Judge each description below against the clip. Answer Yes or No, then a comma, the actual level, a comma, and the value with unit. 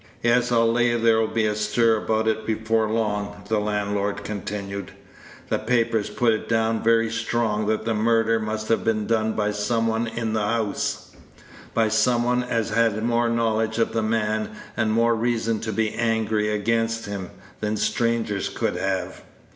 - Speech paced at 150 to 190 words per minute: Yes, average, 170 wpm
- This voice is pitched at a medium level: No, low, 110 Hz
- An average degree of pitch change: No, narrow, 1.3 semitones